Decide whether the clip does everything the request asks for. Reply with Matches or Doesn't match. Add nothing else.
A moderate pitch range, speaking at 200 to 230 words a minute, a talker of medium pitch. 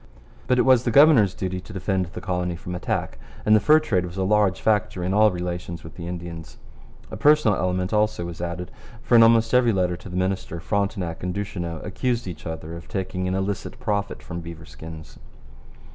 Doesn't match